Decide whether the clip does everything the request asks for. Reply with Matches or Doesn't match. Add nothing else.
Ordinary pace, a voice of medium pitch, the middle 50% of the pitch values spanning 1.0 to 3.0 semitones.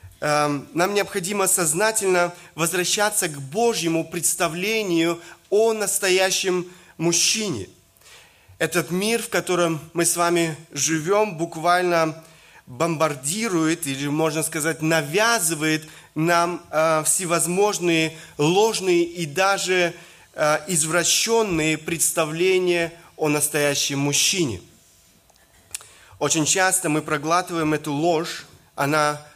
Doesn't match